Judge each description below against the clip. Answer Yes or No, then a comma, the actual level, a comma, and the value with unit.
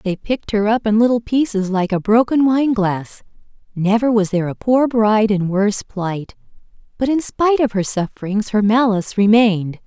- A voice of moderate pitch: No, high, 215 Hz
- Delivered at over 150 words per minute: Yes, average, 175 wpm